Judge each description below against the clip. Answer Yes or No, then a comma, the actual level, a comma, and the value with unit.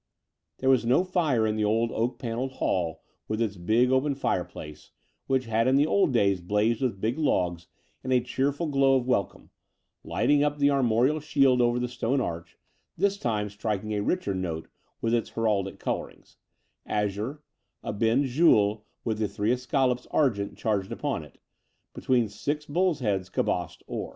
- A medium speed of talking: Yes, average, 170 wpm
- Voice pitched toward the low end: Yes, low, 120 Hz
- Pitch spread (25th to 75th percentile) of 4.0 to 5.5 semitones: Yes, average, 4.6 semitones